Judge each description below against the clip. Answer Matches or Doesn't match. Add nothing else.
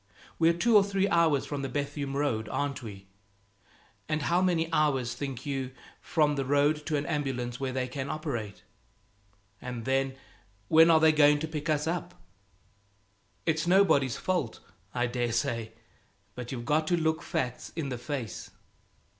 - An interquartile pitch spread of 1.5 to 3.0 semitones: Doesn't match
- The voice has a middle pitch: Matches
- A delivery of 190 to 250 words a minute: Doesn't match